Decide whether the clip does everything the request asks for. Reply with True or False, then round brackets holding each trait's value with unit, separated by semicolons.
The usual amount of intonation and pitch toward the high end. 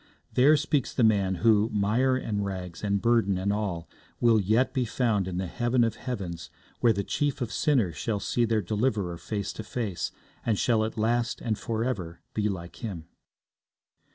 False (3.7 semitones; 110 Hz)